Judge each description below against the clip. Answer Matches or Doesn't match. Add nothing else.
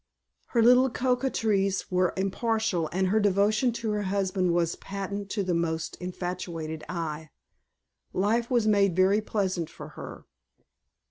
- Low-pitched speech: Doesn't match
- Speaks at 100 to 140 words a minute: Matches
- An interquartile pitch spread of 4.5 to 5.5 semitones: Doesn't match